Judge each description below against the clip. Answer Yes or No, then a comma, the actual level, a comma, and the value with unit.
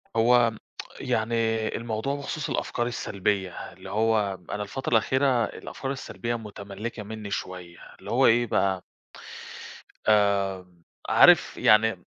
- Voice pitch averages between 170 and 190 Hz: No, low, 110 Hz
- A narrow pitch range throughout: No, average, 3.2 semitones